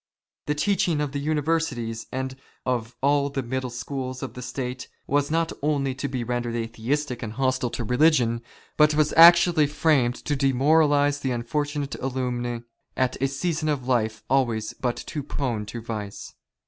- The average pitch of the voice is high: No, low, 135 Hz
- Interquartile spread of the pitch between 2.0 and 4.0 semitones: Yes, average, 3.3 semitones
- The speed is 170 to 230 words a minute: No, average, 160 wpm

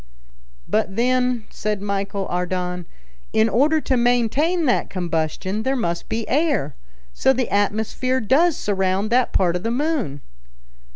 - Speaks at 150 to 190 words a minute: No, slow, 135 wpm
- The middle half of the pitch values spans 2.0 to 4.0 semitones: No, average, 5.2 semitones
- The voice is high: Yes, high, 220 Hz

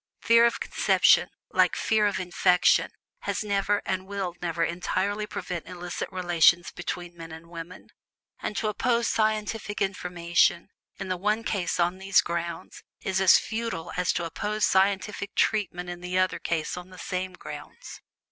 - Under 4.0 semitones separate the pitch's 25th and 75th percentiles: Yes, average, 2.7 semitones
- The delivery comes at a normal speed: Yes, average, 155 wpm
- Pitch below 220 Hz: Yes, medium, 185 Hz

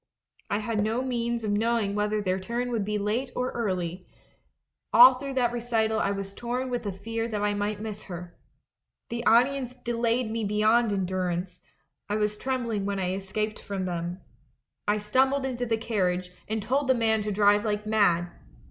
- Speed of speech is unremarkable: Yes, average, 185 wpm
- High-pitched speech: Yes, high, 215 Hz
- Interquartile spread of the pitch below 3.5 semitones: Yes, average, 3.0 semitones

